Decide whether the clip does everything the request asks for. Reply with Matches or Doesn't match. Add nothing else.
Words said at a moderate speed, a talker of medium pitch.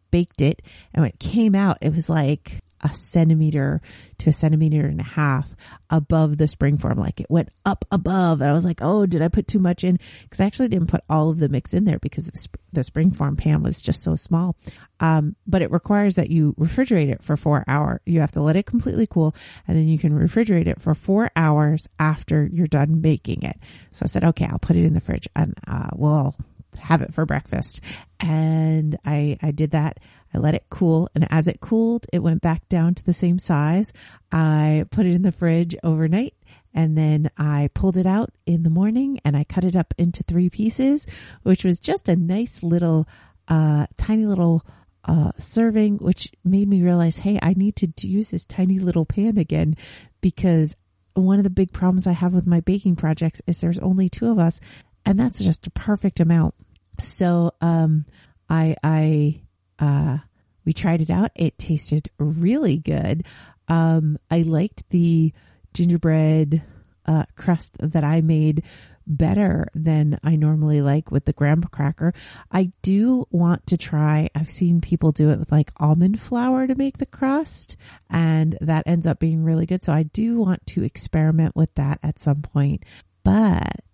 Matches